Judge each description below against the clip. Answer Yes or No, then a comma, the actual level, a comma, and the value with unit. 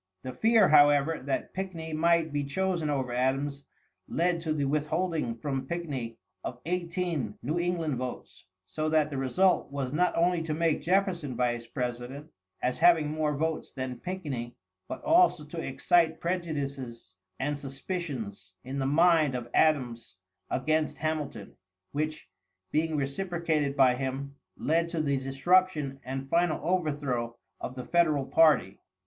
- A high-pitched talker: No, medium, 150 Hz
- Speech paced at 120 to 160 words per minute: Yes, average, 140 wpm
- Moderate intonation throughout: Yes, average, 4.1 semitones